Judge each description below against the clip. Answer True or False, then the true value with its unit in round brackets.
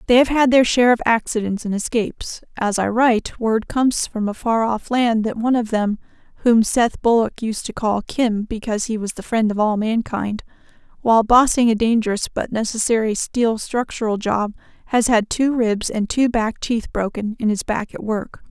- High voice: True (225 Hz)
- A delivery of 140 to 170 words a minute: False (200 wpm)